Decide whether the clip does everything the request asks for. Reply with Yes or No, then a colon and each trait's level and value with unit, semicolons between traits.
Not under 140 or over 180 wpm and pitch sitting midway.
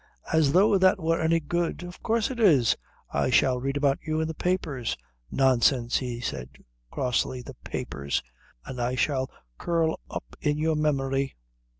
Yes: average, 165 wpm; medium, 145 Hz